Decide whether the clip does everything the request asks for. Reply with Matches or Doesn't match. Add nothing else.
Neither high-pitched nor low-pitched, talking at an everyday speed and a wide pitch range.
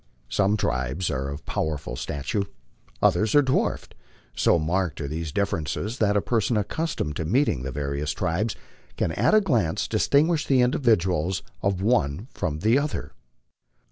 Doesn't match